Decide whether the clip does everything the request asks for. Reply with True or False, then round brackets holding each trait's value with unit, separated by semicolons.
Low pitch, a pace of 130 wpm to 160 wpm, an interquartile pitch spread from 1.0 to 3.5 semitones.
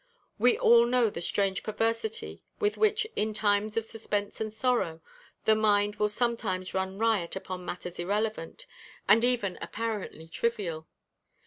False (215 Hz; 140 wpm; 3.2 semitones)